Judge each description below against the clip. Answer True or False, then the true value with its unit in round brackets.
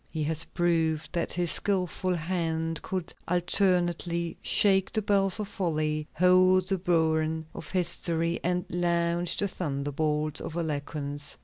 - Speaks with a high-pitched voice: False (170 Hz)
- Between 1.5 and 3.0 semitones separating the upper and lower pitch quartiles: True (2.4 semitones)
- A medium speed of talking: False (130 wpm)